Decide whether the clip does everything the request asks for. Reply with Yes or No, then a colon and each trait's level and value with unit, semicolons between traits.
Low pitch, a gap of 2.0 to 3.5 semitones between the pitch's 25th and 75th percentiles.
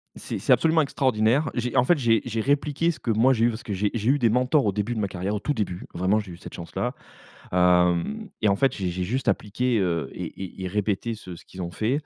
No: low, 110 Hz; average, 5.1 semitones